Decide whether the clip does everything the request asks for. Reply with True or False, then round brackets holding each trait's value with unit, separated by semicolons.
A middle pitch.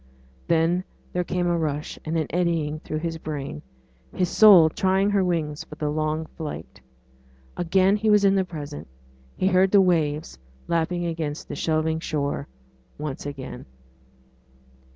True (165 Hz)